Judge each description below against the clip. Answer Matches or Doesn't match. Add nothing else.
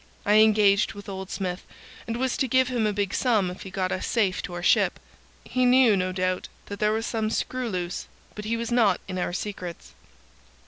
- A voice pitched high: Matches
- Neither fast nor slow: Doesn't match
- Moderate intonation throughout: Matches